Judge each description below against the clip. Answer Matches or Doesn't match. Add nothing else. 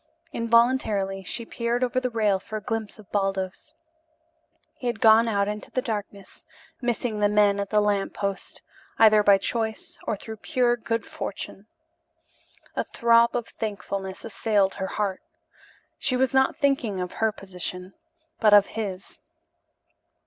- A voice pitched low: Doesn't match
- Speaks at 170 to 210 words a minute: Doesn't match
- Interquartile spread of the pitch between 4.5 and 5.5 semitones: Doesn't match